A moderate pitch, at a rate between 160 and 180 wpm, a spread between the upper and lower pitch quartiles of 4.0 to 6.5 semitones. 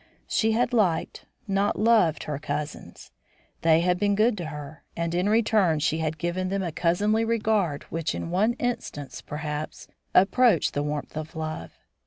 Yes: medium, 175 Hz; average, 165 wpm; wide, 5.4 semitones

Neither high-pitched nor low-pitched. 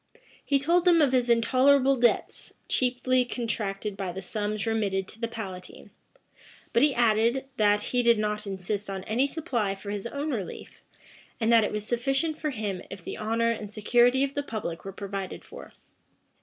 No: high, 225 Hz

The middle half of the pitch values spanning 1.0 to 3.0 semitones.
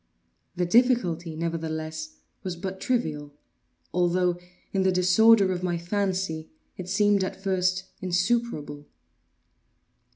Yes: narrow, 2.6 semitones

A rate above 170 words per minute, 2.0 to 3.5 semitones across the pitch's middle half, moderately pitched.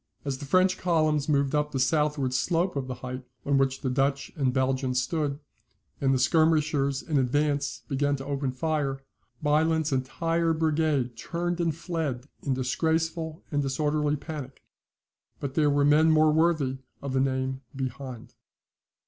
No: average, 155 wpm; average, 2.9 semitones; medium, 145 Hz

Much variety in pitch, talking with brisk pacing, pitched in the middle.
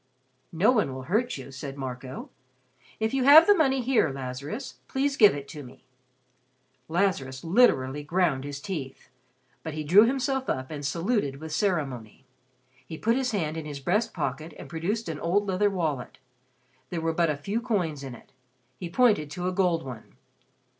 No: wide, 7.1 semitones; average, 175 wpm; medium, 165 Hz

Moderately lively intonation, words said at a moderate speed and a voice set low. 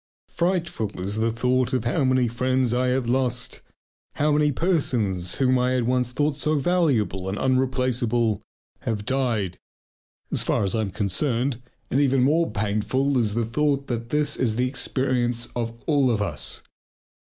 Yes: average, 3.1 semitones; average, 160 wpm; low, 125 Hz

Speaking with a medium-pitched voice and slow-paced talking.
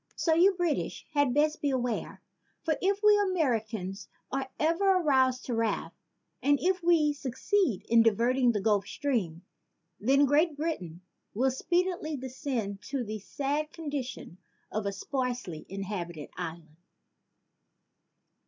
No: very high, 265 Hz; slow, 125 wpm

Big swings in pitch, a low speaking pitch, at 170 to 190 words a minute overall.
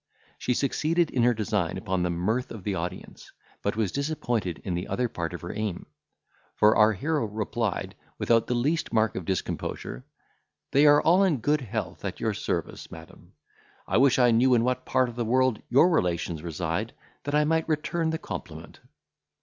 Yes: wide, 6.6 semitones; low, 115 Hz; average, 185 wpm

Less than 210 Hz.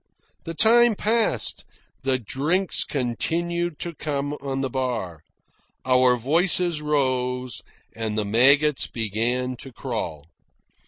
Yes: low, 135 Hz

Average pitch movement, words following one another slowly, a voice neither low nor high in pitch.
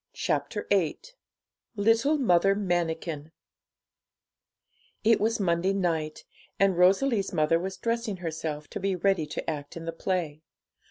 Yes: average, 3.7 semitones; slow, 125 wpm; medium, 180 Hz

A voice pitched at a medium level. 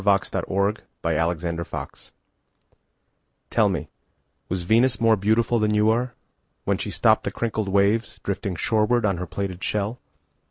No: low, 100 Hz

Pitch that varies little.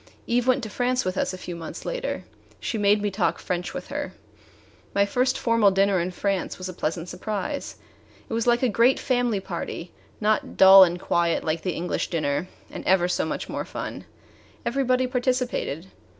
No: wide, 5.4 semitones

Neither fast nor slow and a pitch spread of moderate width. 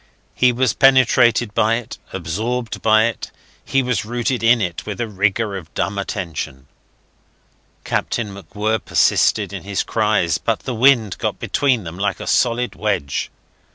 Yes: average, 155 wpm; average, 3.6 semitones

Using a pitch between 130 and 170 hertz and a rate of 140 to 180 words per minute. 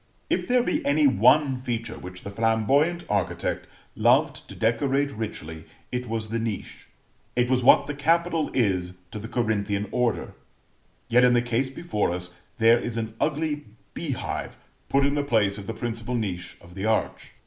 No: low, 115 Hz; average, 170 wpm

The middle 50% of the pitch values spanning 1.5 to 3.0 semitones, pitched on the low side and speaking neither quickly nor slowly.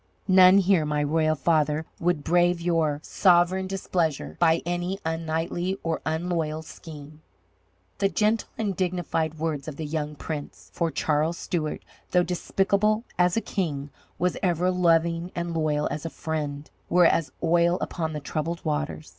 No: narrow, 2.4 semitones; medium, 165 Hz; average, 150 wpm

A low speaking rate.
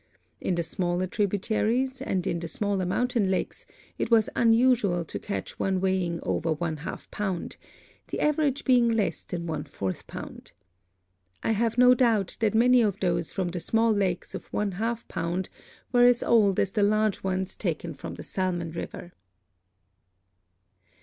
No: average, 165 wpm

